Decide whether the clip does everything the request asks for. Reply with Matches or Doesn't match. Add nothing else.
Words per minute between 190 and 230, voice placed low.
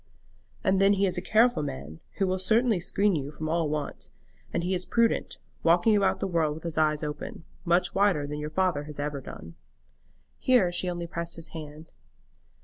Doesn't match